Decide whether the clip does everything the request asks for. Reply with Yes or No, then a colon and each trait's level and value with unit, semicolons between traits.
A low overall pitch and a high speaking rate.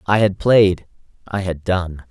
No: very low, 95 Hz; average, 145 wpm